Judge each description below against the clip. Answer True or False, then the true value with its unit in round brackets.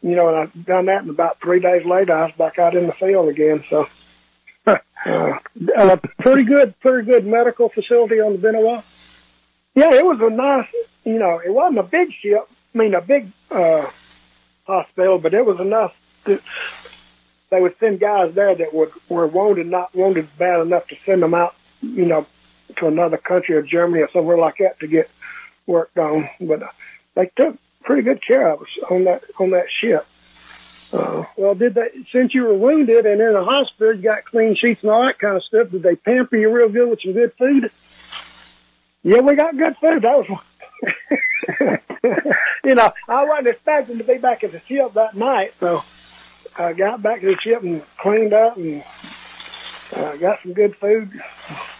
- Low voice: False (200 Hz)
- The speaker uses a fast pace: False (195 wpm)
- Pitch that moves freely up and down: True (5.8 semitones)